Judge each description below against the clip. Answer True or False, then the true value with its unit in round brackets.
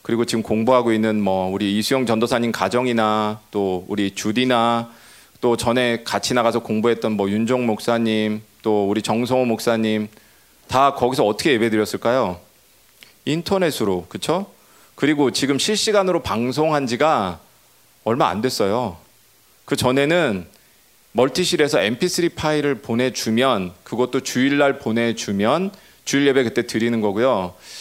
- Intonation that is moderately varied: True (3.9 semitones)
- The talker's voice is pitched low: True (120 Hz)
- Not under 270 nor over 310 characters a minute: True (300 characters per minute)